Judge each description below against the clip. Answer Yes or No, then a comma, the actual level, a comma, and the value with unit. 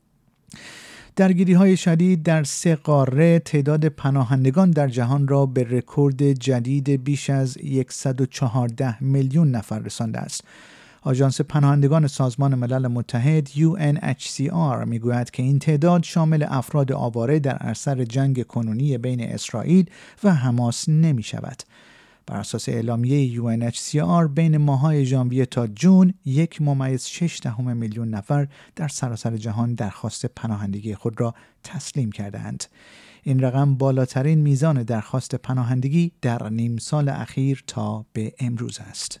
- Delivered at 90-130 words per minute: Yes, average, 120 wpm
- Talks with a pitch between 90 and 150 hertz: Yes, low, 135 Hz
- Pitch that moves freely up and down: No, average, 3.8 semitones